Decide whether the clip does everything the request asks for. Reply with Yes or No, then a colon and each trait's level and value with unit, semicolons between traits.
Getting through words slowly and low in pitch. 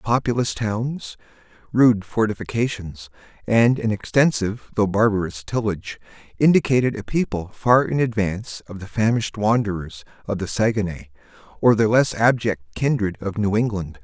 Yes: slow, 130 wpm; low, 110 Hz